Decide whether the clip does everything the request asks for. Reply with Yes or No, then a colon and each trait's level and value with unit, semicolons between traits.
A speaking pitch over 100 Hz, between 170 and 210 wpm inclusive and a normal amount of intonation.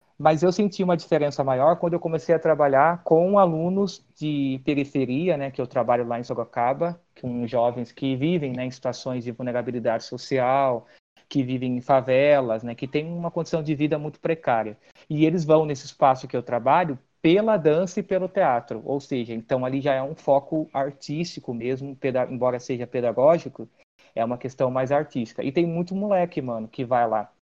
Yes: medium, 140 Hz; fast, 185 wpm; average, 4.4 semitones